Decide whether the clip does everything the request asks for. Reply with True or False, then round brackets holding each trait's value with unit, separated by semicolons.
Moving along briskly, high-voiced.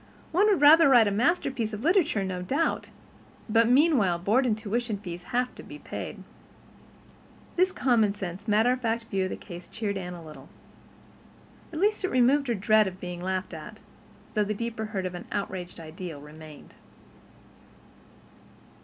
False (160 wpm; 215 Hz)